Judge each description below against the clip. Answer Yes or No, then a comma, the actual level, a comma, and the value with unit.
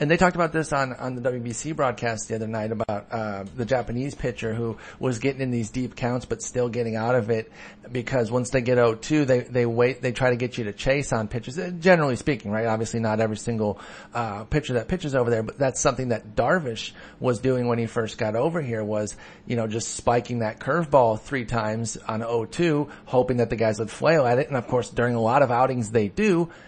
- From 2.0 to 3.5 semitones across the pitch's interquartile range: Yes, average, 2.8 semitones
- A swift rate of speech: Yes, fast, 240 wpm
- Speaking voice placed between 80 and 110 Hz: No, low, 120 Hz